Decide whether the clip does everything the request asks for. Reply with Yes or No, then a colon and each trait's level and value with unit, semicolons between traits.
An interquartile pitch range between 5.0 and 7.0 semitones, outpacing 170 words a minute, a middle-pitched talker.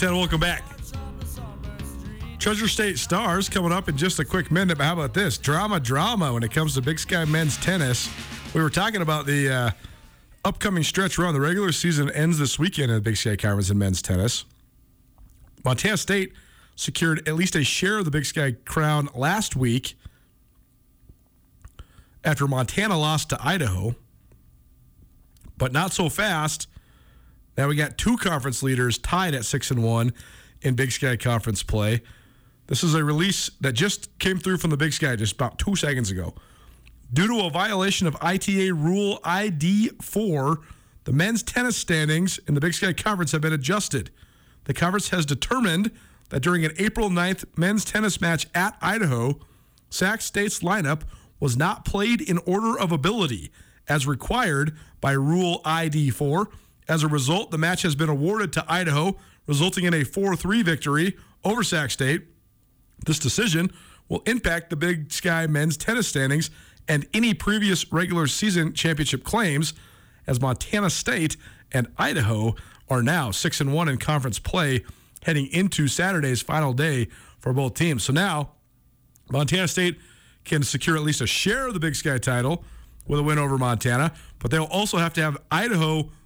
No: wide, 5.6 semitones; average, 165 wpm; medium, 155 Hz